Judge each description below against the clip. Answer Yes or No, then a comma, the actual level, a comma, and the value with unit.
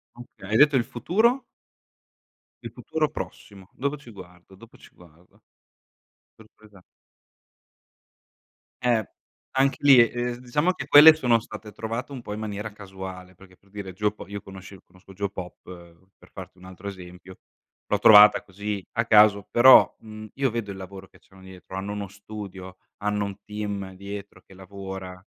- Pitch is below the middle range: Yes, low, 100 Hz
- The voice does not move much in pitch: No, average, 3.4 semitones